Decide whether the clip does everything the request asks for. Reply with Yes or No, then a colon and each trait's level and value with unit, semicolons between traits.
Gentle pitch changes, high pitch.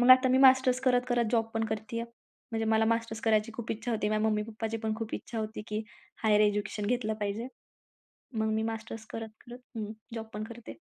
Yes: narrow, 1.4 semitones; high, 225 Hz